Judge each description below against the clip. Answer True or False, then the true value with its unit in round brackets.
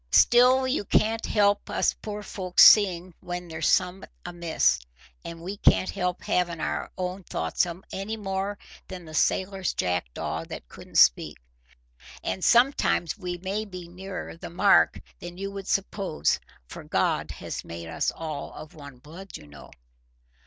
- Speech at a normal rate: True (150 wpm)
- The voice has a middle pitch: True (180 Hz)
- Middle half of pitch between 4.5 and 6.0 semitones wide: False (3.3 semitones)